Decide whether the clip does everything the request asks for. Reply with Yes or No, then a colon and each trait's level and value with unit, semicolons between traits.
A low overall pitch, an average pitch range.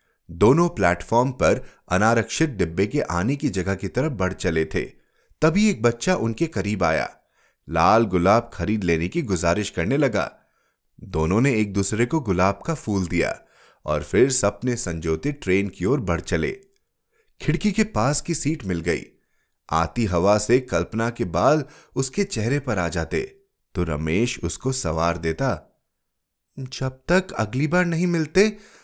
No: low, 115 Hz; wide, 8.6 semitones